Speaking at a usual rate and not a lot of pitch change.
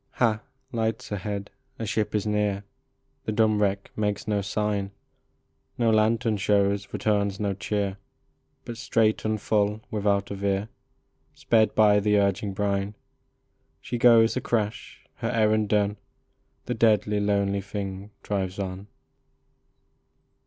No: slow, 130 wpm; narrow, 1.5 semitones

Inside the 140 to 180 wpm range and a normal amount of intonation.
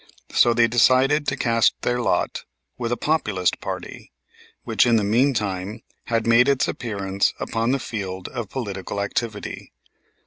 Yes: average, 145 wpm; average, 3.3 semitones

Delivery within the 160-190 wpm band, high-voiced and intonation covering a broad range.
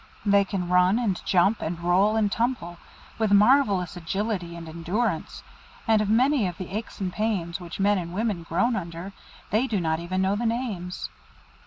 No: average, 180 wpm; high, 195 Hz; average, 3.8 semitones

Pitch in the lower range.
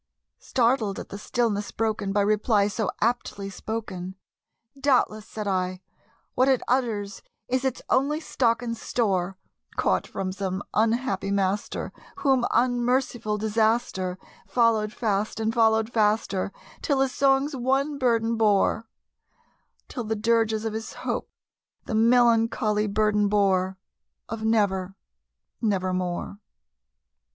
No: high, 220 Hz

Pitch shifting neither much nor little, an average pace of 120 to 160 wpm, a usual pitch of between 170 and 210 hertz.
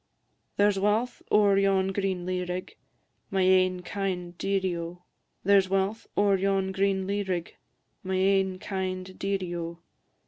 No: narrow, 1.2 semitones; average, 150 wpm; high, 190 Hz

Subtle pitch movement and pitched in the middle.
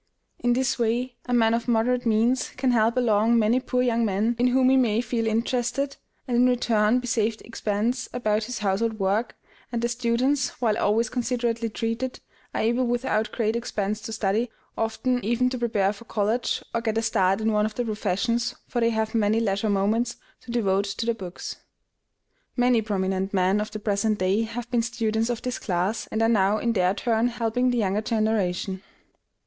No: narrow, 2.3 semitones; high, 225 Hz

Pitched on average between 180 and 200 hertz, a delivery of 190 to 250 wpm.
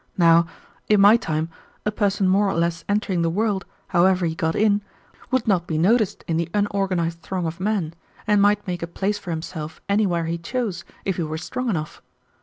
Yes: medium, 185 Hz; average, 200 wpm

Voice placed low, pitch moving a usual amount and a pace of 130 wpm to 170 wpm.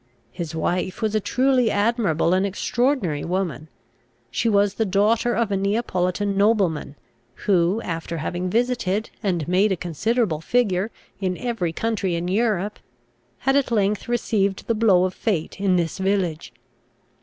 No: high, 195 Hz; average, 4.0 semitones; average, 145 wpm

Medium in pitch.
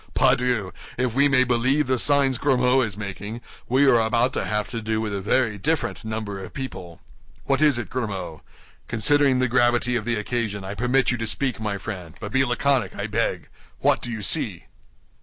No: low, 120 Hz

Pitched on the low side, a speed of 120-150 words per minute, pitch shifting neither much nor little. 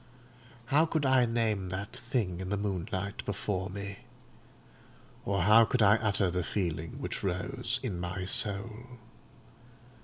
Yes: low, 100 Hz; average, 140 wpm; average, 3.8 semitones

